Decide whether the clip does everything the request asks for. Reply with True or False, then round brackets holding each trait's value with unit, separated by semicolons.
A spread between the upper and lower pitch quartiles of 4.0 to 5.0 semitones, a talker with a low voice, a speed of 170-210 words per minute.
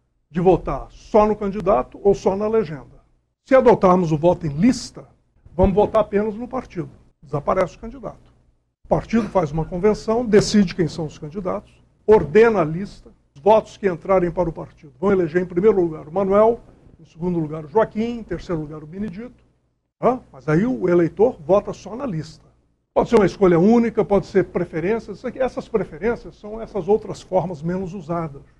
False (4.5 semitones; 190 Hz; 180 wpm)